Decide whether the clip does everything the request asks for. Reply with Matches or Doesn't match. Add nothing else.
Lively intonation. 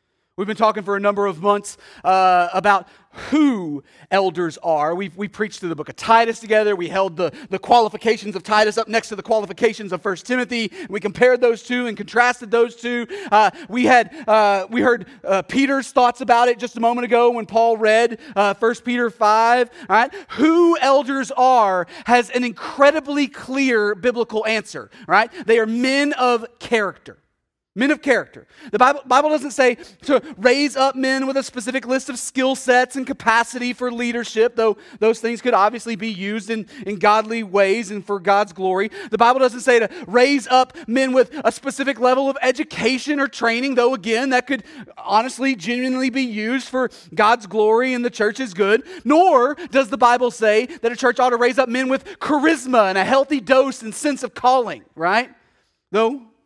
Doesn't match